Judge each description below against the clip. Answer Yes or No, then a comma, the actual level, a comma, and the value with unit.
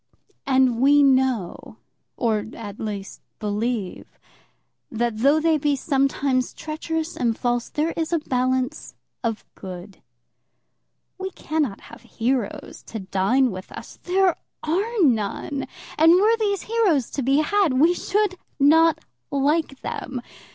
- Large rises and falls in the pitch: Yes, wide, 5.7 semitones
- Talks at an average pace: No, slow, 130 wpm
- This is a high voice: Yes, very high, 270 Hz